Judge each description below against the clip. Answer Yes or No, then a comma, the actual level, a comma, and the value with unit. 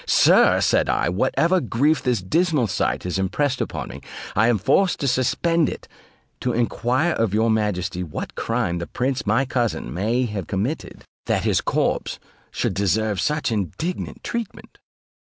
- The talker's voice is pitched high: No, low, 115 Hz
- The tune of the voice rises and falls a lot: Yes, wide, 6.3 semitones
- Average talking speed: Yes, average, 155 wpm